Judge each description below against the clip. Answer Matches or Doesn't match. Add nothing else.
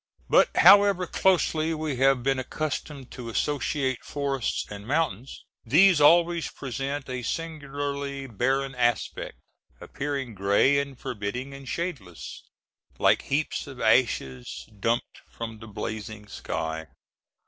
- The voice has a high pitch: Doesn't match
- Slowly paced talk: Matches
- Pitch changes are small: Doesn't match